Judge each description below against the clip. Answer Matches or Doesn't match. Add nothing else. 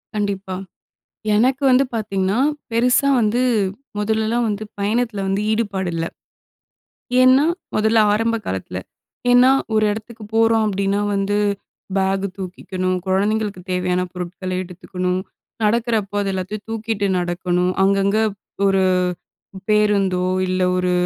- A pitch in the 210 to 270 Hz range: Doesn't match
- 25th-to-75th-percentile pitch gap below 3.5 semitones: Matches